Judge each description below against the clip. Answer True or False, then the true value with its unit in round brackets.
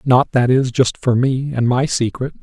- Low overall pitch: True (125 Hz)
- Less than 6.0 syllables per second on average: True (4.4 syllables/s)